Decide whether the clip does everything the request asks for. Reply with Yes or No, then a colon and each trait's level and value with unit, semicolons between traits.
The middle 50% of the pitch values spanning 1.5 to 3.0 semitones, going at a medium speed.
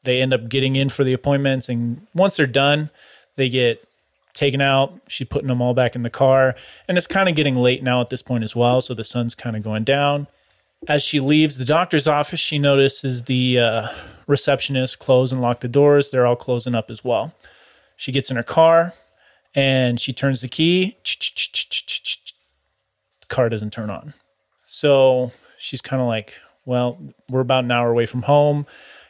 Yes: average, 2.7 semitones; average, 190 wpm